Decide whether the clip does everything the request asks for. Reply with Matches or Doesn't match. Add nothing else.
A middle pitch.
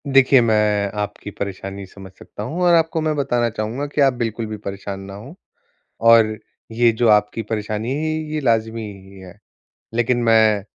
Doesn't match